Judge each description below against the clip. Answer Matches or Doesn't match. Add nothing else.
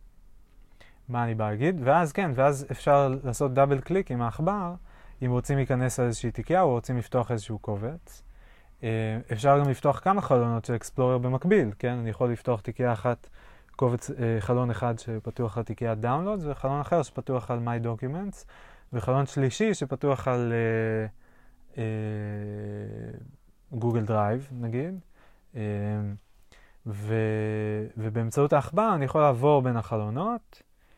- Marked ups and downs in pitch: Doesn't match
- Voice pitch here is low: Matches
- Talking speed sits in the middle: Matches